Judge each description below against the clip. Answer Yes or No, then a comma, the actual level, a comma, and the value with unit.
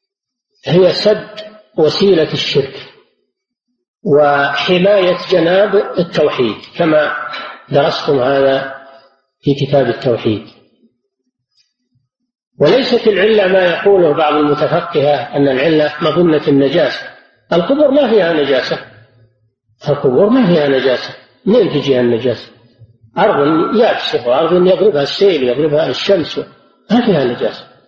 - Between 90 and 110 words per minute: Yes, average, 95 wpm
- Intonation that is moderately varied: No, wide, 6.9 semitones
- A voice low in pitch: No, medium, 150 Hz